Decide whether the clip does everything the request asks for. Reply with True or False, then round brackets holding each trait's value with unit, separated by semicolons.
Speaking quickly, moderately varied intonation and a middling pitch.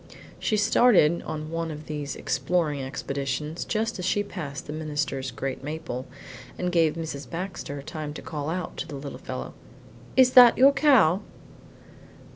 False (155 wpm; 4.4 semitones; 155 Hz)